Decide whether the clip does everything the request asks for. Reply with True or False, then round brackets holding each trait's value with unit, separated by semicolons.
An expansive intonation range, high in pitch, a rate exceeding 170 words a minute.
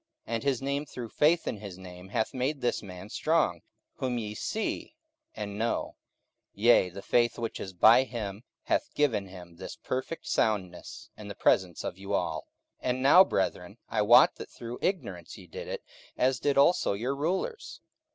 False (5.9 semitones; 115 Hz; 180 wpm)